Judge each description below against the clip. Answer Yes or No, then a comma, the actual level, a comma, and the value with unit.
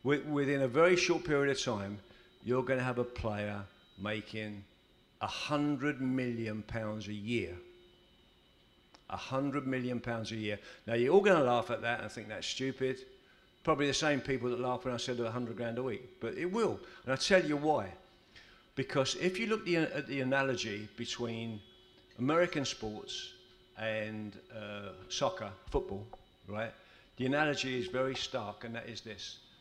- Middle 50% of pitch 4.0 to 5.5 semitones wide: Yes, average, 4.7 semitones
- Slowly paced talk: No, average, 170 wpm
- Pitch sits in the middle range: No, low, 125 Hz